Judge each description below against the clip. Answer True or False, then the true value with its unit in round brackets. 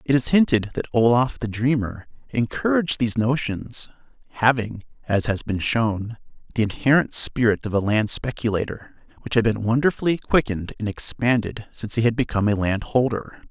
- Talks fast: False (155 wpm)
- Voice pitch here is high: False (115 Hz)